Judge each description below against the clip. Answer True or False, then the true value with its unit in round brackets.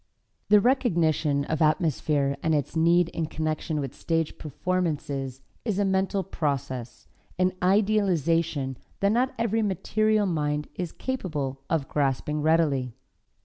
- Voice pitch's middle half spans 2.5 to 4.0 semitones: False (4.7 semitones)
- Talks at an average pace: False (125 wpm)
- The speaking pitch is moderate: True (160 Hz)